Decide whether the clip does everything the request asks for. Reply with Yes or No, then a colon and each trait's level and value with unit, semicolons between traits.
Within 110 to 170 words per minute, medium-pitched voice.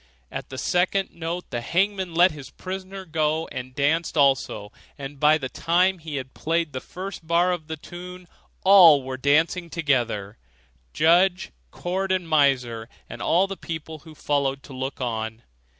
Yes: average, 165 wpm; medium, 160 Hz